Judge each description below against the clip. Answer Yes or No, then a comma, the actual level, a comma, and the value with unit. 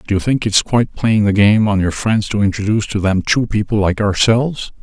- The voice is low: Yes, low, 105 Hz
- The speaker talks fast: Yes, fast, 235 wpm